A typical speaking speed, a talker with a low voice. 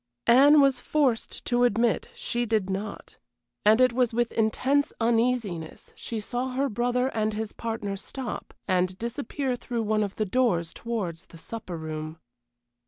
No: average, 155 wpm; high, 230 Hz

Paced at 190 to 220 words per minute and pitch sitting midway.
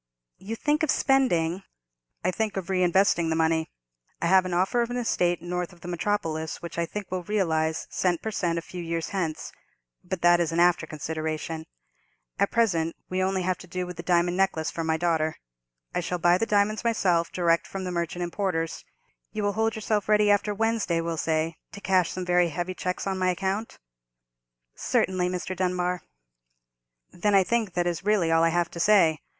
Yes: average, 195 wpm; medium, 180 Hz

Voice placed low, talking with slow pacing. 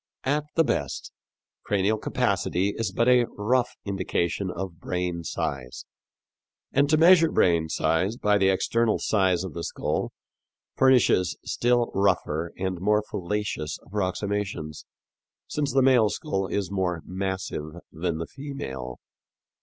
Yes: very low, 95 Hz; slow, 130 wpm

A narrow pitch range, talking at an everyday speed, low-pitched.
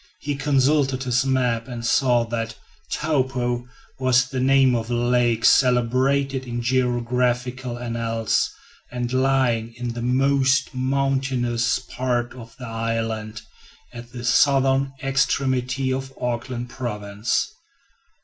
No: narrow, 1.9 semitones; slow, 115 wpm; low, 125 Hz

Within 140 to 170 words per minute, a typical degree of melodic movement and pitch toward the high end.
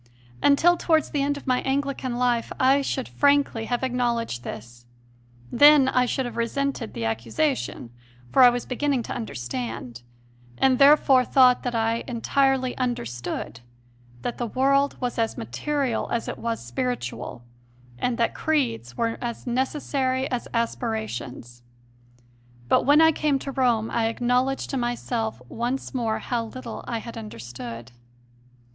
Yes: average, 145 wpm; average, 3.5 semitones; high, 245 Hz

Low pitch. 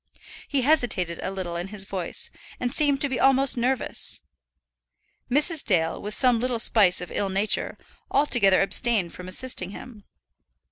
No: high, 220 Hz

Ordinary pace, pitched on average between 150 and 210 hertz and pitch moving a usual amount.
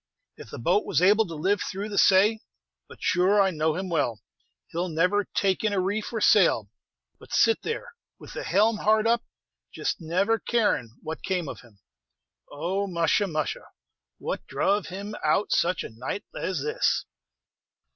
Yes: average, 175 wpm; high, 190 Hz; average, 4.0 semitones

